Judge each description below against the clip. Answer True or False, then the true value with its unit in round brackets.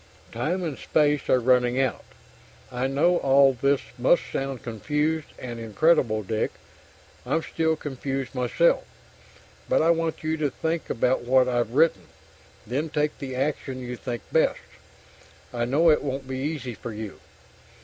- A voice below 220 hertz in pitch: True (135 Hz)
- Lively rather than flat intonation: False (3.8 semitones)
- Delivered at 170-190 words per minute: False (150 wpm)